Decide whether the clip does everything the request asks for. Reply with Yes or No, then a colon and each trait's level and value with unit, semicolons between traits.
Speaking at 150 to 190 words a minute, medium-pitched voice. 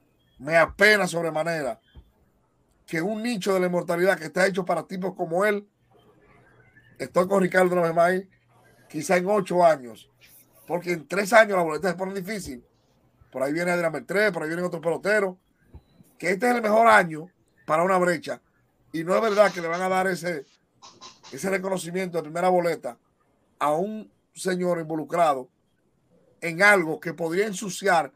Yes: average, 160 wpm; medium, 180 Hz